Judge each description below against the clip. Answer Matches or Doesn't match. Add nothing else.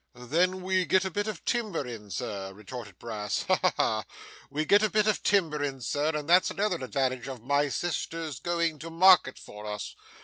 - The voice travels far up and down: Matches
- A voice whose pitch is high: Doesn't match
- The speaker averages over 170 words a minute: Matches